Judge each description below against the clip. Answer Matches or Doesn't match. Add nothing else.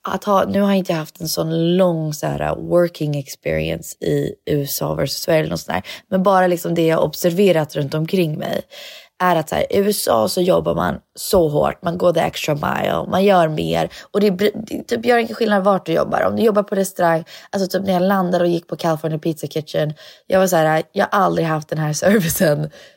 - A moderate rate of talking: Doesn't match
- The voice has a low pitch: Doesn't match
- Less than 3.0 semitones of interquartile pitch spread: Doesn't match